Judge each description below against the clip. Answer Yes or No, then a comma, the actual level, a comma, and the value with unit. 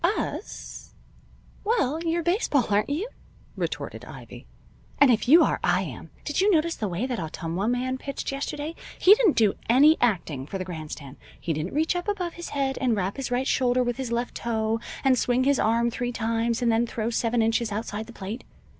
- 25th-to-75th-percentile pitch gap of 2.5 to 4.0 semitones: No, average, 4.6 semitones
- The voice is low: No, high, 245 Hz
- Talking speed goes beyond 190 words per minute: Yes, average, 200 wpm